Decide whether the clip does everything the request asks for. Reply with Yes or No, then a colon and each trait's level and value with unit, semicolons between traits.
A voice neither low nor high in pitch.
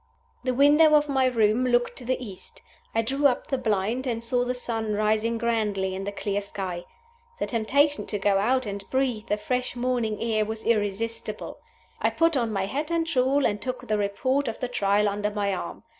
No: high, 230 Hz